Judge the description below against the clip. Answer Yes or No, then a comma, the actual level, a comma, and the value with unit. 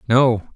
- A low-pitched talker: Yes, low, 120 Hz